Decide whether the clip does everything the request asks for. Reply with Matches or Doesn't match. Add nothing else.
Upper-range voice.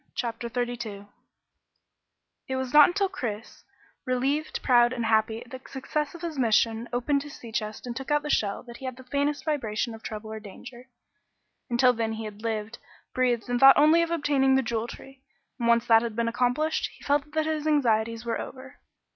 Matches